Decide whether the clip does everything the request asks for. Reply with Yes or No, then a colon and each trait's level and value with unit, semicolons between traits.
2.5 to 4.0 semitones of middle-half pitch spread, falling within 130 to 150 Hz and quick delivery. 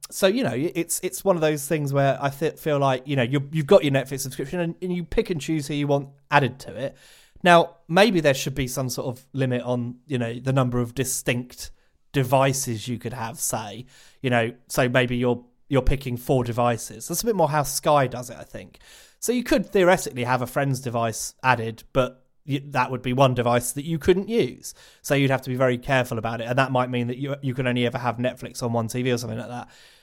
Yes: average, 3.7 semitones; low, 135 Hz; fast, 245 wpm